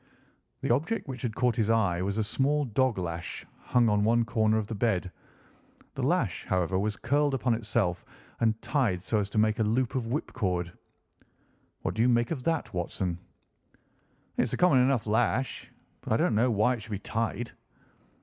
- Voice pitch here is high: No, low, 115 Hz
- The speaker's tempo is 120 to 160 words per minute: No, average, 190 wpm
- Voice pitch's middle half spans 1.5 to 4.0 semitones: Yes, average, 3.5 semitones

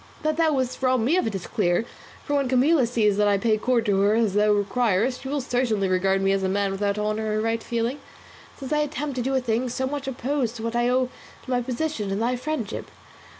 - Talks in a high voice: Yes, high, 235 Hz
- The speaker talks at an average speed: No, fast, 250 wpm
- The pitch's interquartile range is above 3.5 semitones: Yes, average, 4.0 semitones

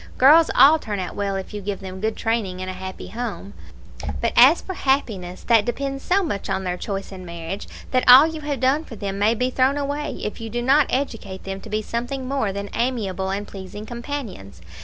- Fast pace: Yes, fast, 220 wpm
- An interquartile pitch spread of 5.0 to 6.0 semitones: Yes, wide, 5.5 semitones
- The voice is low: No, high, 220 Hz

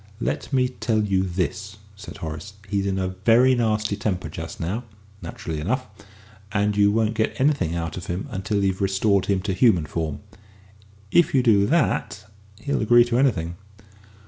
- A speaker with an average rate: Yes, average, 170 wpm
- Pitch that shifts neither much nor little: Yes, average, 3.7 semitones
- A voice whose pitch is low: Yes, low, 100 Hz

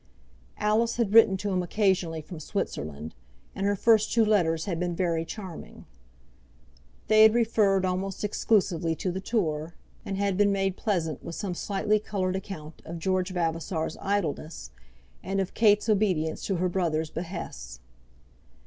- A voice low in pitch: No, medium, 185 Hz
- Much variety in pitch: No, average, 3.8 semitones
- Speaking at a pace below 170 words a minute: Yes, average, 150 wpm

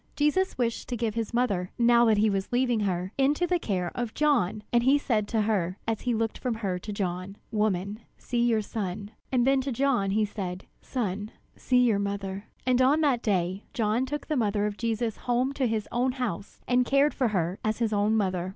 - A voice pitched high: Yes, high, 220 Hz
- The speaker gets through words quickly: Yes, fast, 215 wpm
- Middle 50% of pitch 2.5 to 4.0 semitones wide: Yes, average, 3.7 semitones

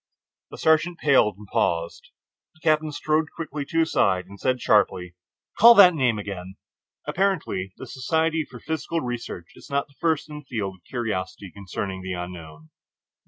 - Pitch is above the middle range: No, low, 125 Hz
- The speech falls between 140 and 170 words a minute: Yes, average, 165 wpm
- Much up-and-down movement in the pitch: Yes, wide, 9.0 semitones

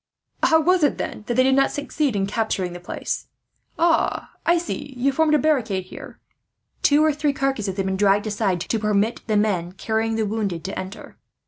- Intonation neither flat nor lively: No, wide, 6.5 semitones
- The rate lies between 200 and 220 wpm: Yes, fast, 205 wpm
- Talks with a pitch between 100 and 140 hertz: No, high, 220 Hz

